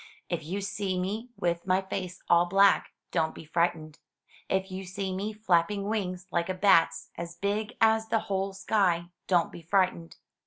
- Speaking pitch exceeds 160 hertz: Yes, high, 190 Hz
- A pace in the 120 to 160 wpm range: No, average, 170 wpm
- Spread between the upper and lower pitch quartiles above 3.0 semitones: No, narrow, 2.6 semitones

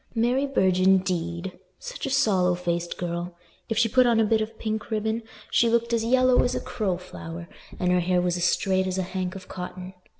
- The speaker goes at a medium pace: No, fast, 210 wpm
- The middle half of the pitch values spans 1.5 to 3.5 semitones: No, average, 4.2 semitones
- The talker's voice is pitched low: No, high, 190 Hz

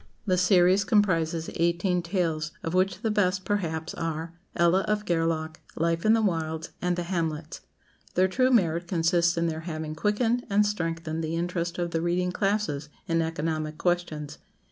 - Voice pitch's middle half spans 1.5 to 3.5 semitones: Yes, narrow, 2.4 semitones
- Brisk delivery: No, average, 165 wpm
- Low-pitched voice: No, medium, 170 Hz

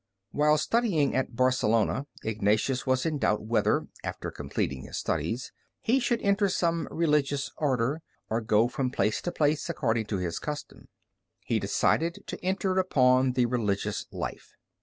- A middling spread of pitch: No, wide, 6.1 semitones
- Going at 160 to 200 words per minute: No, average, 150 wpm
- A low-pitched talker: Yes, low, 130 Hz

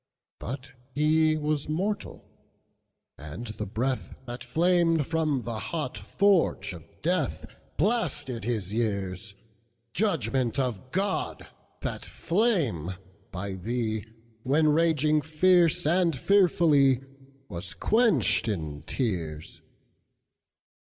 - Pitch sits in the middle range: No, low, 130 Hz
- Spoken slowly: Yes, slow, 85 wpm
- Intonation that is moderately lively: No, wide, 6.8 semitones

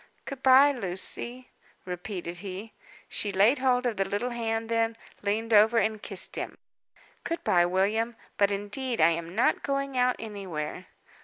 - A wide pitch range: No, average, 4.2 semitones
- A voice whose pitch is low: No, high, 220 Hz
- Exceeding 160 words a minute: No, average, 155 wpm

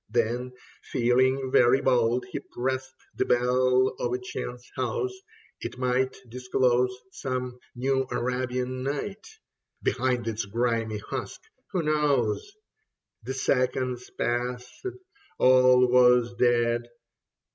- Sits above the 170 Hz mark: No, low, 125 Hz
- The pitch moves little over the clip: Yes, narrow, 1.2 semitones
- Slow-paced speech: Yes, slow, 105 wpm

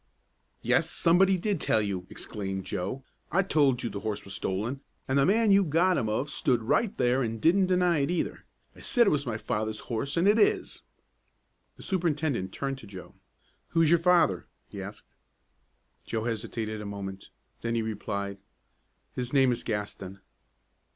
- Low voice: Yes, low, 125 Hz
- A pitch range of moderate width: No, wide, 7.9 semitones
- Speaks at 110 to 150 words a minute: No, average, 175 wpm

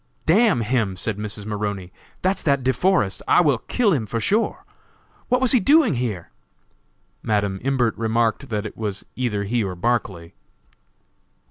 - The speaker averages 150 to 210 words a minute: Yes, average, 155 wpm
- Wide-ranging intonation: Yes, wide, 5.9 semitones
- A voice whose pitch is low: Yes, low, 115 Hz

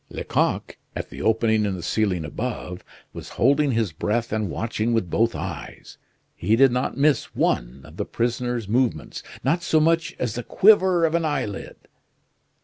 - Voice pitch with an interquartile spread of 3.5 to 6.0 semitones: Yes, average, 4.7 semitones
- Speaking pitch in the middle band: No, low, 115 Hz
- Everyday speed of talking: Yes, average, 165 wpm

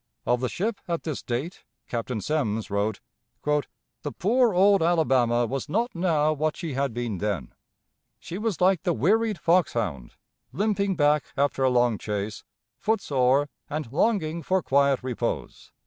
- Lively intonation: Yes, wide, 6.8 semitones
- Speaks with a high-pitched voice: No, medium, 150 Hz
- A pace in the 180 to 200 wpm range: No, average, 155 wpm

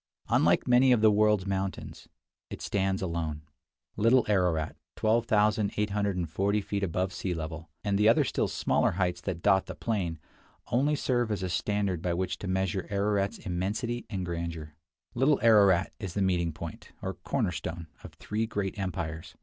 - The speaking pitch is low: Yes, very low, 95 Hz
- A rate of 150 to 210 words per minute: Yes, average, 160 wpm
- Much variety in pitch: No, average, 3.4 semitones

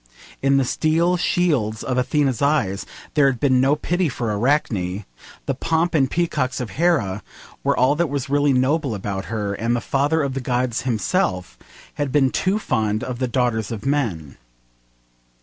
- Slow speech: No, average, 170 wpm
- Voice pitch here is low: Yes, low, 130 Hz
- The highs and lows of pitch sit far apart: No, average, 4.7 semitones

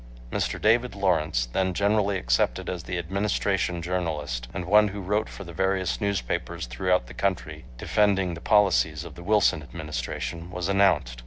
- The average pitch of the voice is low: Yes, very low, 90 Hz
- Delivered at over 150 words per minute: Yes, average, 160 wpm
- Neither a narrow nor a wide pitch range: Yes, average, 4.0 semitones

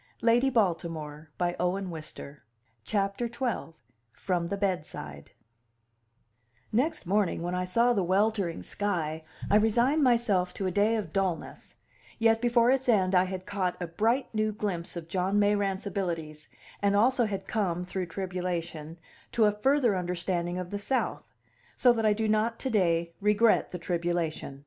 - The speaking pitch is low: No, high, 195 Hz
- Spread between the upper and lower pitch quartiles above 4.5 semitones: No, average, 4.1 semitones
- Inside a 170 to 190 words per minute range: No, average, 160 wpm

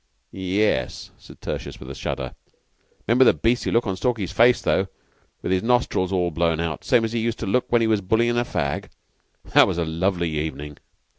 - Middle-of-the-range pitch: No, very low, 95 Hz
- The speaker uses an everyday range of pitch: No, wide, 5.7 semitones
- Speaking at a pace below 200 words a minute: No, fast, 205 wpm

